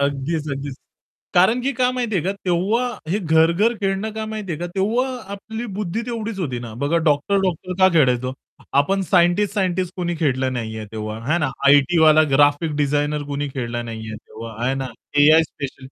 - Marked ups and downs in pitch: Yes, wide, 5.9 semitones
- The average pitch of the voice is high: No, medium, 160 Hz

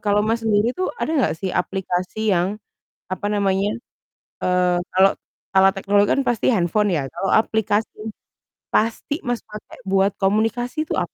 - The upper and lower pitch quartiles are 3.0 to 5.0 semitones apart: No, narrow, 2.6 semitones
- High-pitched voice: Yes, high, 205 Hz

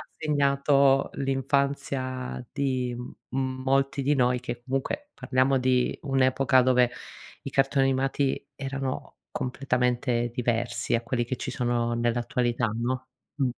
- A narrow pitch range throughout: Yes, narrow, 1.8 semitones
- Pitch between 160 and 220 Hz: No, low, 130 Hz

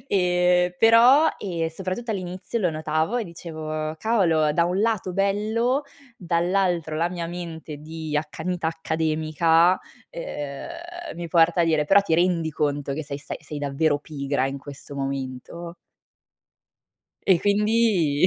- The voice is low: No, medium, 170 Hz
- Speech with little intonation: No, average, 3.3 semitones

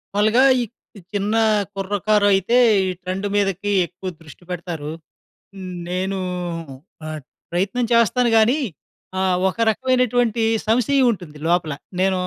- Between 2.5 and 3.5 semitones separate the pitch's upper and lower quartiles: No, average, 4.0 semitones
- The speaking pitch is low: No, high, 200 Hz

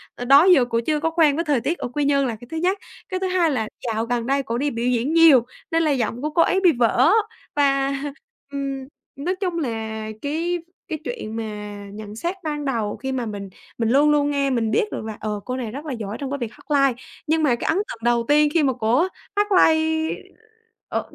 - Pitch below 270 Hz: No, very high, 275 Hz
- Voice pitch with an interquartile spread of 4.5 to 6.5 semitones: Yes, average, 5.0 semitones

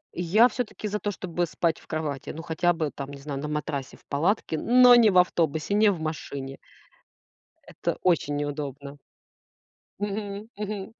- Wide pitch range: Yes, wide, 5.9 semitones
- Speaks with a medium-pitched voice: Yes, medium, 165 Hz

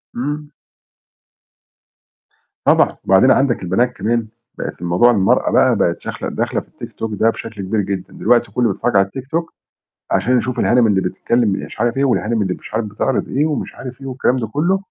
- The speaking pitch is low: Yes, low, 120 Hz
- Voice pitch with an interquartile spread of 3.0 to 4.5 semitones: Yes, average, 3.8 semitones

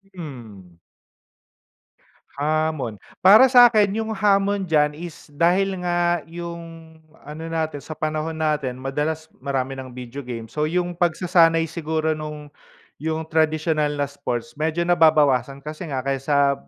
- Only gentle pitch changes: No, average, 3.2 semitones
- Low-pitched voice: No, medium, 155 Hz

